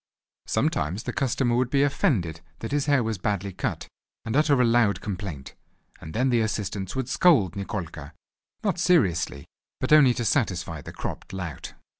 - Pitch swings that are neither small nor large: No, wide, 6.5 semitones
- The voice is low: Yes, low, 110 Hz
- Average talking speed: Yes, average, 170 wpm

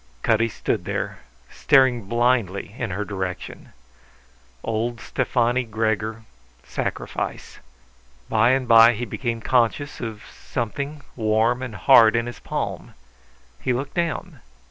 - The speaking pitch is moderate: No, low, 115 Hz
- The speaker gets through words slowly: Yes, slow, 120 wpm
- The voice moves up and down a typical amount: No, narrow, 2.2 semitones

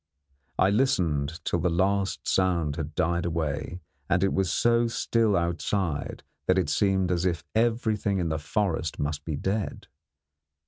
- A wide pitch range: No, average, 3.7 semitones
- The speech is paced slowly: No, average, 150 wpm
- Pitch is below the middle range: Yes, very low, 90 Hz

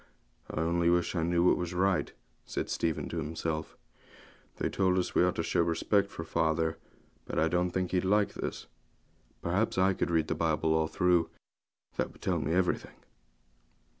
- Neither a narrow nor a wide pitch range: No, narrow, 1.9 semitones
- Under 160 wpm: No, average, 185 wpm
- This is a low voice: Yes, very low, 85 Hz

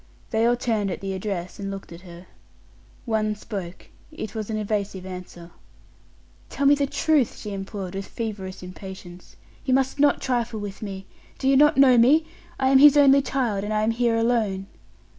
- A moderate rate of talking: Yes, average, 185 wpm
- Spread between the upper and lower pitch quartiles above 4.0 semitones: Yes, average, 5.0 semitones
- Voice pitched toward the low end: No, high, 215 Hz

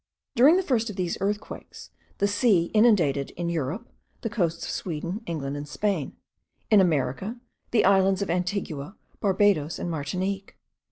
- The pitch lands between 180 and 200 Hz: Yes, high, 190 Hz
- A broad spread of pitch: No, average, 4.2 semitones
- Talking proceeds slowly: No, average, 150 wpm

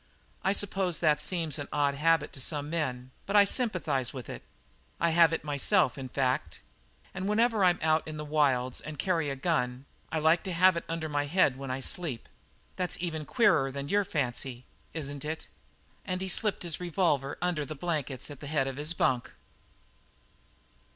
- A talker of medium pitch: Yes, medium, 155 Hz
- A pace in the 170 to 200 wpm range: Yes, average, 185 wpm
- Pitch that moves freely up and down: No, average, 4.3 semitones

